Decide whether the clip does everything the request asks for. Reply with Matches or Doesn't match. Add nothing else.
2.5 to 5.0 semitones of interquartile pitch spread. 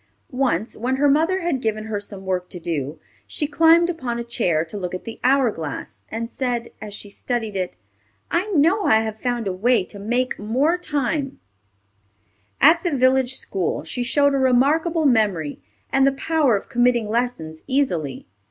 Doesn't match